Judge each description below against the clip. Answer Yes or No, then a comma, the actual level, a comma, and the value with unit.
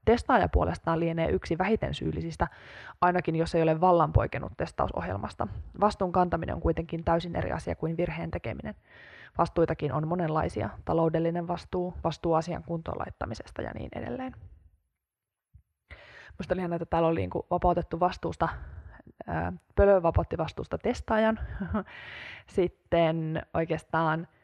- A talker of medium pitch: Yes, medium, 165 Hz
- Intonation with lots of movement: Yes, wide, 8.5 semitones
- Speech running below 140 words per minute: Yes, average, 120 wpm